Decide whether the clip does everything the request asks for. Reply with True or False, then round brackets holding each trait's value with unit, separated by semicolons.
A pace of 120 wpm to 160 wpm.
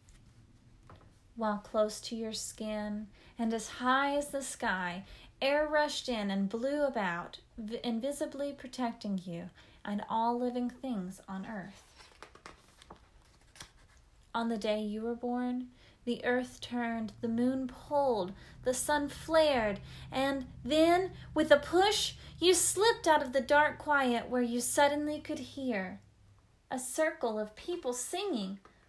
True (135 wpm)